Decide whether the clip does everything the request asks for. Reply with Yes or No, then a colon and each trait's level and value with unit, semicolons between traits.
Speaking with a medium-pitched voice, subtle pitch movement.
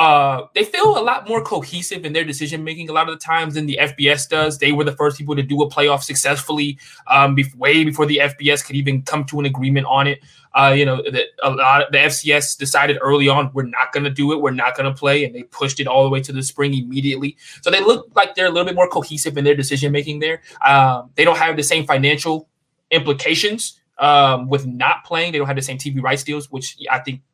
Yes: medium, 145 Hz; narrow, 2.2 semitones